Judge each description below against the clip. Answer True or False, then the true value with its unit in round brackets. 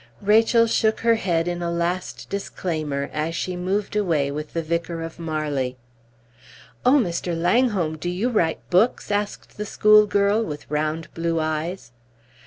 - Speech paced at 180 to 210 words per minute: False (150 wpm)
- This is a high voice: False (175 Hz)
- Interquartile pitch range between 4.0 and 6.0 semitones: True (4.6 semitones)